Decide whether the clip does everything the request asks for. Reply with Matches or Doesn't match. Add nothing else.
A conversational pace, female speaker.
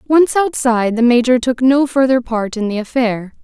Matches